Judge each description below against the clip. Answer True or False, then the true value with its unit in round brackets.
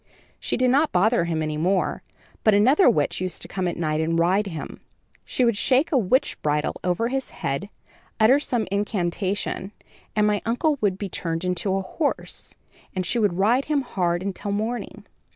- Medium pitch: False (200 Hz)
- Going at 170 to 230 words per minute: True (185 wpm)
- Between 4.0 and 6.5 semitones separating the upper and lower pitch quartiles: True (5.2 semitones)